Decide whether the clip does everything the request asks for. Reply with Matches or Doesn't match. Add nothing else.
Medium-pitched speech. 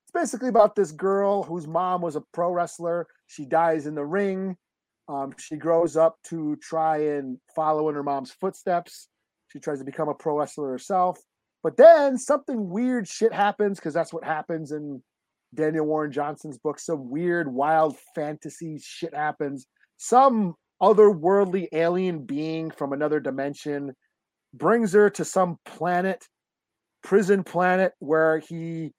Matches